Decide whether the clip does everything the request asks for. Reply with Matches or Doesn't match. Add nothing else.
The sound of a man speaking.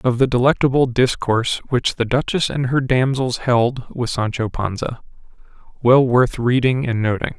Matches